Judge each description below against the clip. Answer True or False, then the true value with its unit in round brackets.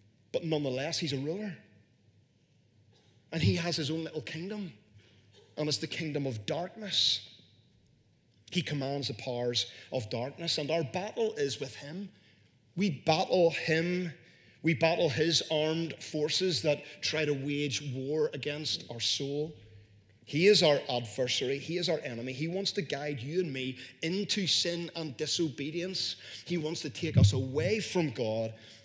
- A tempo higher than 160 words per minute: False (150 wpm)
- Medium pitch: True (150 Hz)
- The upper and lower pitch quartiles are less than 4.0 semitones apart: False (4.9 semitones)